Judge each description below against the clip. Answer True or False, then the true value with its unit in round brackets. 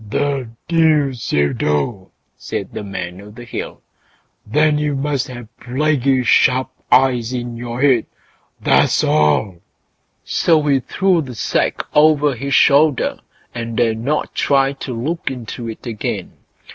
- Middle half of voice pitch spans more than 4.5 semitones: False (4.0 semitones)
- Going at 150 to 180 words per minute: False (140 wpm)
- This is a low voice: True (130 Hz)